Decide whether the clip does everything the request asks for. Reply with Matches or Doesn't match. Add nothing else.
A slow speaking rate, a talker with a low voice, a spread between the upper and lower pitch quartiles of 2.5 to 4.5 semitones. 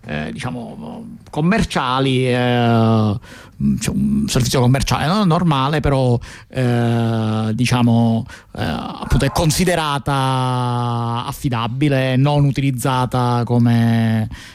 Matches